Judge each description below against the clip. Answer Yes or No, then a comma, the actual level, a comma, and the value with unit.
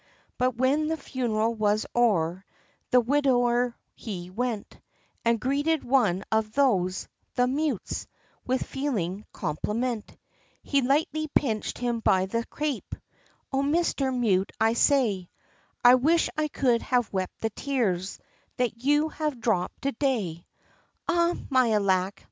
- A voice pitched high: Yes, high, 245 Hz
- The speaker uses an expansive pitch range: No, average, 4.7 semitones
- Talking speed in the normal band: No, slow, 130 wpm